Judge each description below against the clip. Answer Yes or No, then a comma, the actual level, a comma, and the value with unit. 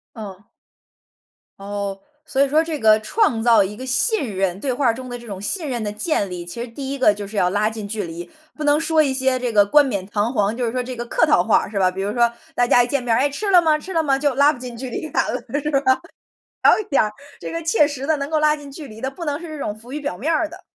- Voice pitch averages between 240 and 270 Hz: Yes, very high, 250 Hz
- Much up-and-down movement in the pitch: Yes, wide, 5.7 semitones